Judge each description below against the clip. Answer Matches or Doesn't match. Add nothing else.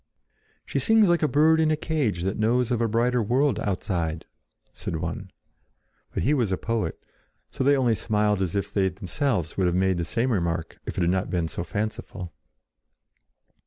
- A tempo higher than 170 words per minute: Matches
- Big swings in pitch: Matches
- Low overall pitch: Matches